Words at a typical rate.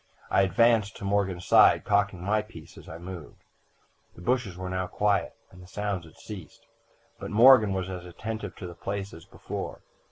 Yes: average, 185 wpm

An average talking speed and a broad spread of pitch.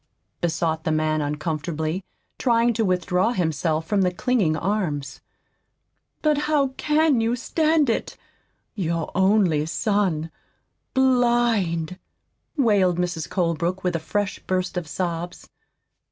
No: slow, 115 wpm; wide, 5.9 semitones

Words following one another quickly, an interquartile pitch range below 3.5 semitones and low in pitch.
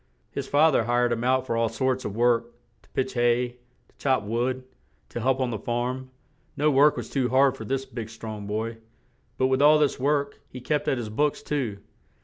Yes: fast, 210 wpm; narrow, 2.4 semitones; low, 130 Hz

